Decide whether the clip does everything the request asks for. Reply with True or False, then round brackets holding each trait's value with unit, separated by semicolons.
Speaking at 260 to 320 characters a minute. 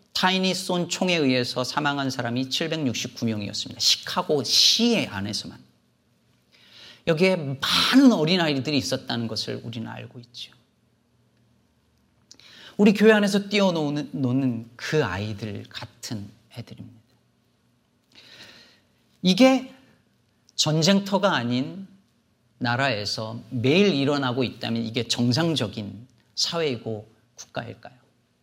False (235 characters per minute)